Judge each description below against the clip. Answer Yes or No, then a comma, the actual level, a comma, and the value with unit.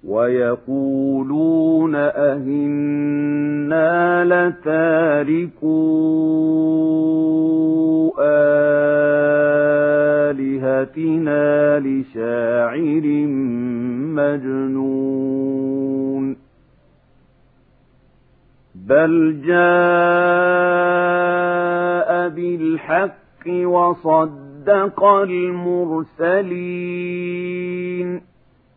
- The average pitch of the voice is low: No, medium, 160 Hz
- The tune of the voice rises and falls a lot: No, average, 3.5 semitones